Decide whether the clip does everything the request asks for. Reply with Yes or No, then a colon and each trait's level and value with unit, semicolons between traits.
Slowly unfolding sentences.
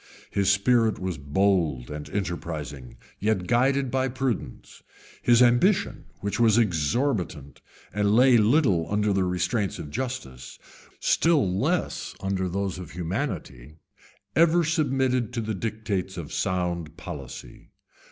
Yes: slow, 125 wpm